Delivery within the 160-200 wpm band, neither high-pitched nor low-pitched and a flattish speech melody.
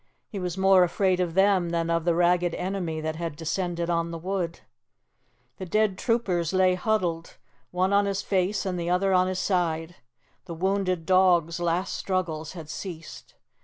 Yes: average, 170 wpm; medium, 180 Hz; narrow, 2.1 semitones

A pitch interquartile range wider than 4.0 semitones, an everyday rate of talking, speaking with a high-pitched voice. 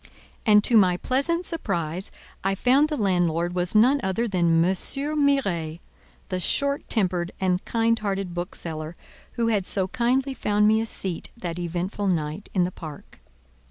Yes: average, 5.0 semitones; average, 160 wpm; high, 195 Hz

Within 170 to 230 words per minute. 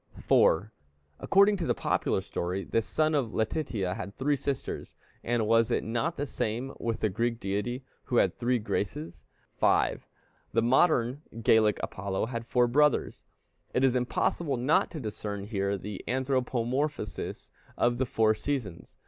No: average, 155 wpm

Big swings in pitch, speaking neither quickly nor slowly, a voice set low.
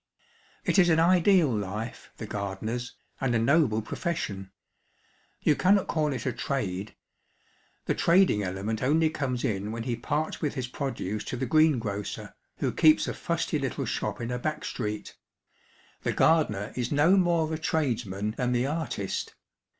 Yes: wide, 6.6 semitones; average, 160 wpm; low, 130 Hz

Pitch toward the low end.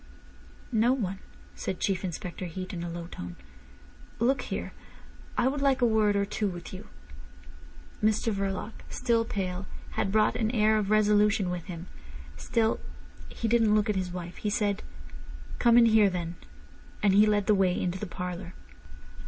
No: high, 205 Hz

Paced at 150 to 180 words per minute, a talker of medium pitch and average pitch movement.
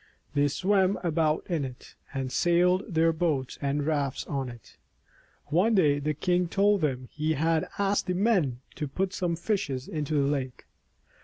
Yes: average, 165 wpm; medium, 155 Hz; average, 4.4 semitones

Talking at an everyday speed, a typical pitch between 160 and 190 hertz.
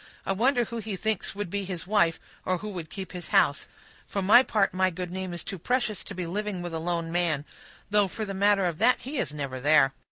No: fast, 245 wpm; medium, 185 Hz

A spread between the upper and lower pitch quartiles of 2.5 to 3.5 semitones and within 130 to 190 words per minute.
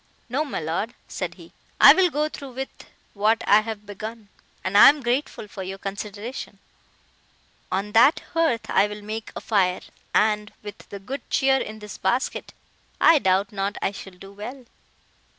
No: average, 4.0 semitones; average, 170 wpm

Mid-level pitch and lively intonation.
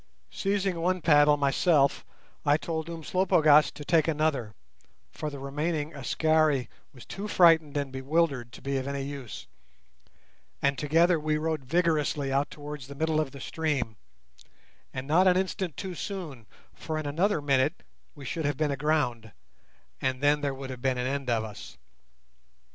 No: medium, 150 Hz; average, 2.9 semitones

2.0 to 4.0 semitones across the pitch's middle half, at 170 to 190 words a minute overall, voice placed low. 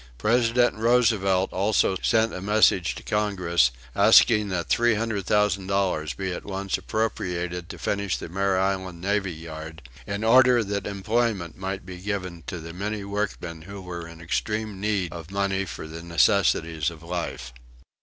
No: average, 3.4 semitones; average, 150 wpm; very low, 95 Hz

